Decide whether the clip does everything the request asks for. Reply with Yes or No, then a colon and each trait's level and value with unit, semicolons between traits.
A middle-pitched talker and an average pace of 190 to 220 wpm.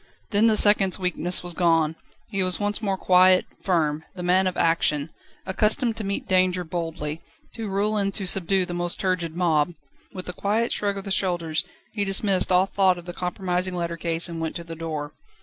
Yes: medium, 180 Hz; average, 195 wpm